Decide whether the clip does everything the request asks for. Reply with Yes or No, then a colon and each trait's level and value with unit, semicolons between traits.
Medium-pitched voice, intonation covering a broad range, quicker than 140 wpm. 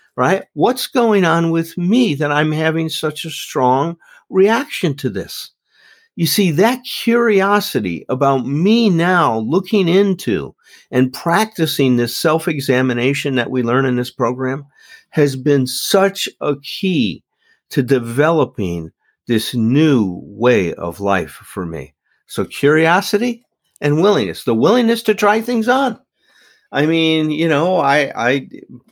No: medium, 155 Hz; wide, 7.3 semitones; slow, 135 wpm